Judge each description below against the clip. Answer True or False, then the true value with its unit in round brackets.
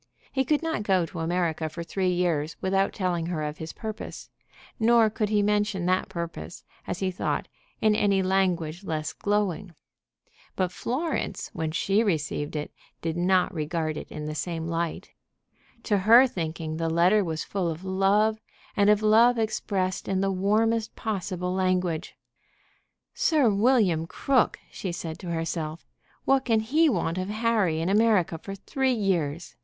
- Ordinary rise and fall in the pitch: True (4.2 semitones)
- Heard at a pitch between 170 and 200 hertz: True (185 Hz)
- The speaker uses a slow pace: False (160 wpm)